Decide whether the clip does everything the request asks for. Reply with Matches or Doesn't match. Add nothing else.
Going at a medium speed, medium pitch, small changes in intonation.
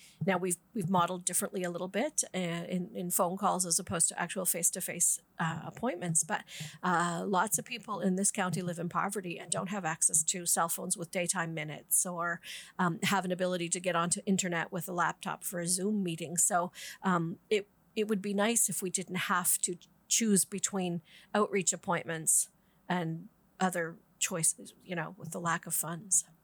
Matches